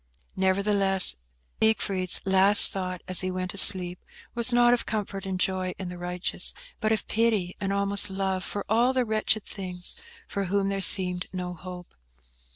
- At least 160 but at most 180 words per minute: Yes, average, 165 wpm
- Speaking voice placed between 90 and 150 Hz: No, high, 195 Hz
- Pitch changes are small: Yes, narrow, 2.1 semitones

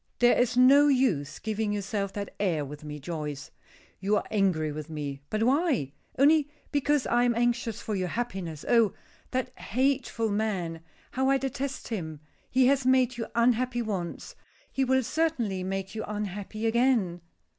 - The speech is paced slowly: No, average, 160 wpm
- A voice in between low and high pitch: No, high, 220 Hz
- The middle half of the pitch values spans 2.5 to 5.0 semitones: No, wide, 5.5 semitones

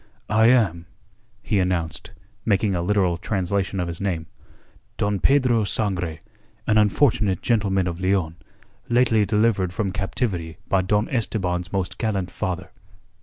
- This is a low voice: Yes, very low, 95 Hz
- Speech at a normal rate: No, slow, 130 wpm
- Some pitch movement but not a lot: Yes, average, 3.2 semitones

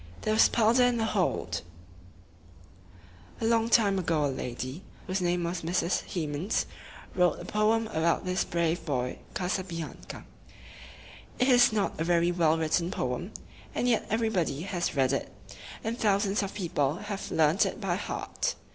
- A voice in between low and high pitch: Yes, medium, 180 Hz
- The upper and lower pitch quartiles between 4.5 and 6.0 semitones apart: Yes, average, 4.8 semitones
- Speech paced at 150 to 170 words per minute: Yes, average, 165 wpm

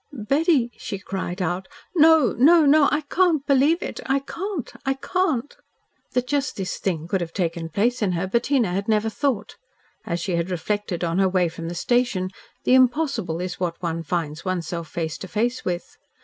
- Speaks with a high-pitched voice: Yes, high, 205 Hz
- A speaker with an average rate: Yes, average, 190 wpm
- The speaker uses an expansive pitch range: Yes, wide, 7.7 semitones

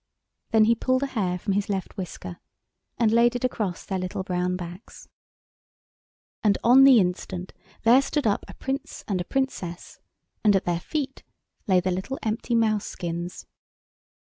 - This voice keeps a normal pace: Yes, average, 165 wpm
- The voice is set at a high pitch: Yes, high, 205 Hz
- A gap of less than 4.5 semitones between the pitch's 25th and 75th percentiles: No, average, 4.8 semitones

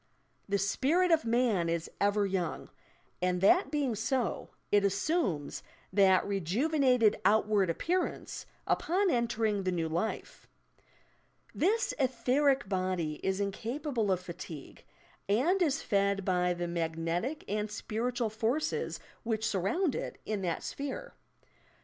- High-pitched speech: Yes, high, 210 Hz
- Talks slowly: Yes, slow, 120 wpm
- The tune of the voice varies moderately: No, wide, 6.1 semitones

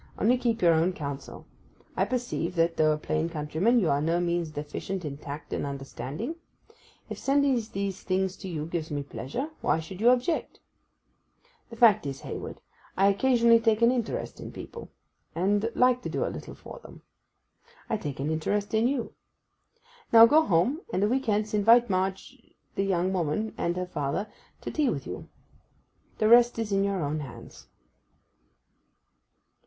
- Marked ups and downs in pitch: Yes, wide, 6.5 semitones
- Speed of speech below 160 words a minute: No, average, 170 wpm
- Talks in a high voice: Yes, high, 195 Hz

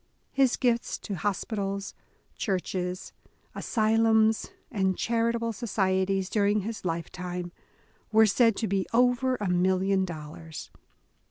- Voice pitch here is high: Yes, high, 200 Hz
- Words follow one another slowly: Yes, slow, 105 wpm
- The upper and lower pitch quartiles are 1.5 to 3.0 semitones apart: No, average, 3.4 semitones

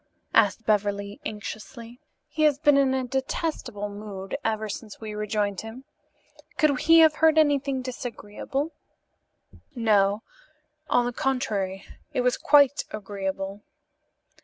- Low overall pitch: No, high, 225 Hz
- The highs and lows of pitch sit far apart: No, average, 4.8 semitones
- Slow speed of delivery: Yes, slow, 120 wpm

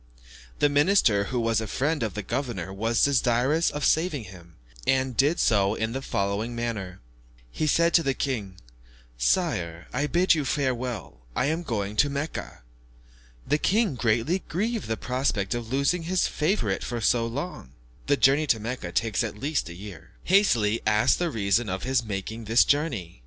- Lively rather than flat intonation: Yes, wide, 5.8 semitones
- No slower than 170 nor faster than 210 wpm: Yes, average, 175 wpm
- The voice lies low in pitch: Yes, low, 120 Hz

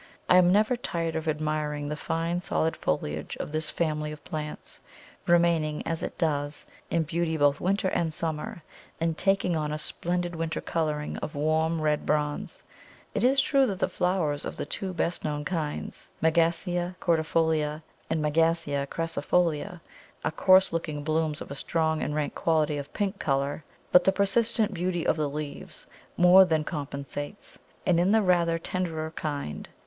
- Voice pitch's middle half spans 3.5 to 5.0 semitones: No, average, 2.7 semitones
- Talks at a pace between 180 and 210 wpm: No, average, 165 wpm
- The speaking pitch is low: No, medium, 160 Hz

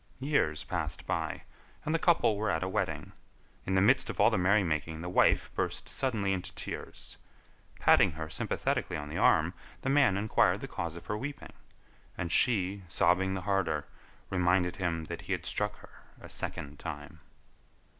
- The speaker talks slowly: No, average, 175 wpm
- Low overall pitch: Yes, very low, 90 Hz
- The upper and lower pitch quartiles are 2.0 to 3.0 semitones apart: No, average, 4.0 semitones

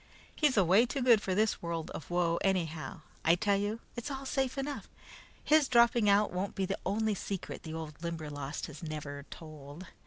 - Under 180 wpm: No, average, 185 wpm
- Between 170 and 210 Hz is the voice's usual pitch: Yes, high, 190 Hz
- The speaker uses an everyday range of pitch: No, wide, 5.9 semitones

